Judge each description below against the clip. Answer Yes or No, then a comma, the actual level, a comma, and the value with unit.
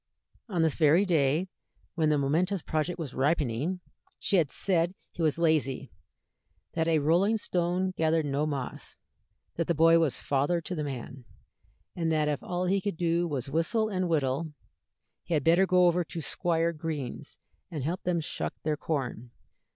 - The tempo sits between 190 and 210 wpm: No, average, 175 wpm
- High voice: No, medium, 165 Hz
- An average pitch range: Yes, average, 3.1 semitones